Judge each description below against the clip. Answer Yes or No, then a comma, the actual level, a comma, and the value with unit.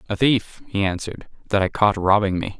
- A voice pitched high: No, low, 100 Hz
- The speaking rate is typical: No, fast, 210 wpm